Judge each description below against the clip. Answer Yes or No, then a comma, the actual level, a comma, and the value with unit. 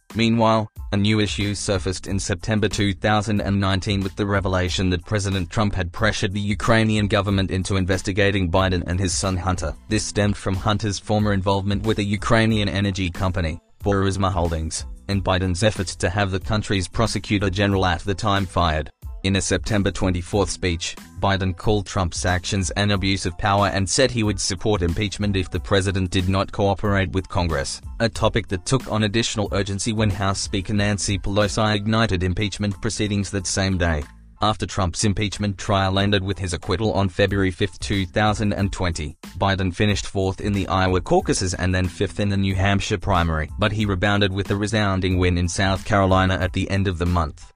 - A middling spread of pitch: No, narrow, 1.9 semitones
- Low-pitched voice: Yes, low, 100 Hz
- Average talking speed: Yes, average, 175 wpm